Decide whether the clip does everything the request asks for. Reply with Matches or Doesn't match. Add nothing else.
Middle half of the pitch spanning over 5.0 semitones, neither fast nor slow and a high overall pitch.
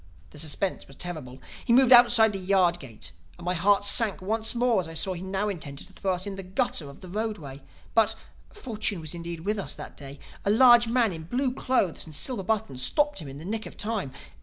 Doesn't match